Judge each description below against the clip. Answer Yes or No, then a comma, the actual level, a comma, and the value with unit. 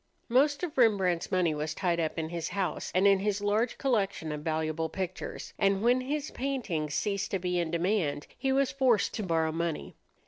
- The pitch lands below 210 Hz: Yes, high, 190 Hz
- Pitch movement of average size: No, wide, 6.1 semitones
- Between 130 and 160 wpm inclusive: No, average, 195 wpm